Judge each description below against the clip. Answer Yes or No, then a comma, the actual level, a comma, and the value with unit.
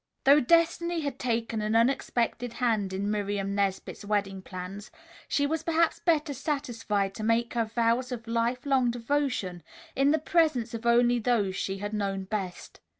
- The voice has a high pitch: Yes, high, 230 Hz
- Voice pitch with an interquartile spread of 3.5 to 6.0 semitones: Yes, average, 4.9 semitones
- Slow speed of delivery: No, average, 160 wpm